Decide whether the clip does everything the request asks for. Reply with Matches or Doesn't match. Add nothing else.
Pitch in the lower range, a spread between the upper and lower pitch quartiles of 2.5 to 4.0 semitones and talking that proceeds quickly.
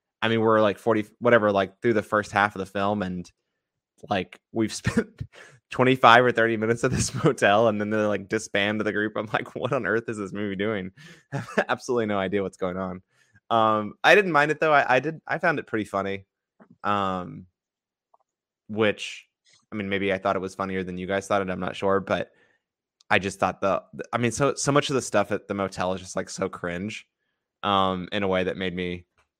Matches